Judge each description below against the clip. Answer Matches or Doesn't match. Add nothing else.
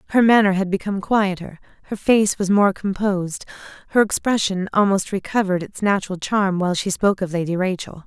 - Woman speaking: Matches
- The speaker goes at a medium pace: Matches